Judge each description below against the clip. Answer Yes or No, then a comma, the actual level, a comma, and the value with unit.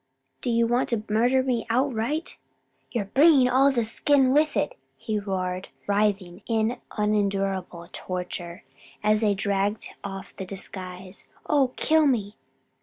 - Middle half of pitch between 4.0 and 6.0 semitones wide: Yes, average, 4.5 semitones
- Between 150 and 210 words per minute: No, slow, 135 wpm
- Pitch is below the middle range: No, high, 215 Hz